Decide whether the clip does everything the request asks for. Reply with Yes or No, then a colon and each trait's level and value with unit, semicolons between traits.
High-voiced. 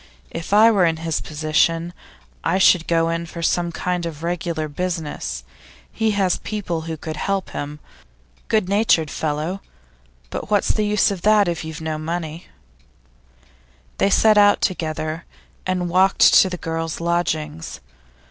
No: medium, 170 Hz